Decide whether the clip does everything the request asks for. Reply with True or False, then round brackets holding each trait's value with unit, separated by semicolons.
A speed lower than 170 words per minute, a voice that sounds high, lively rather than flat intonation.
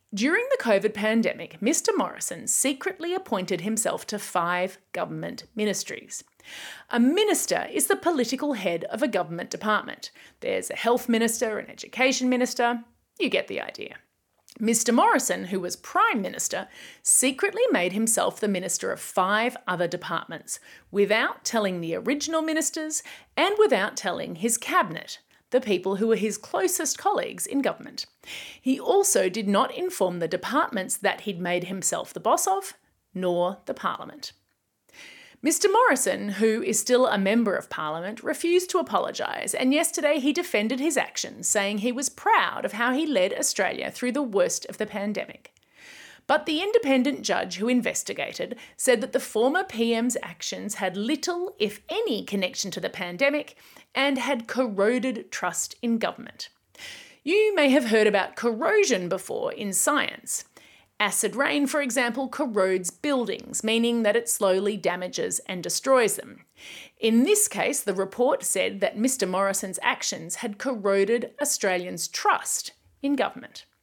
True (150 wpm; 240 Hz; 6.5 semitones)